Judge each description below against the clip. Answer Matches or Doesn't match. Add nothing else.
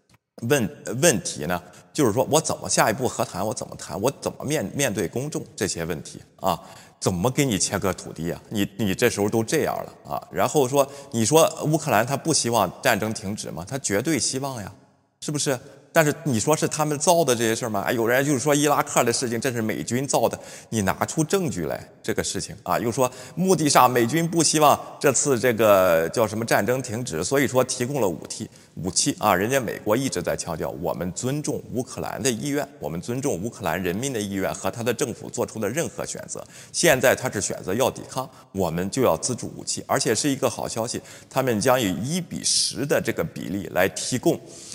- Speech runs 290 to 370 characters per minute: Matches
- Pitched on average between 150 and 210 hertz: Doesn't match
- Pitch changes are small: Doesn't match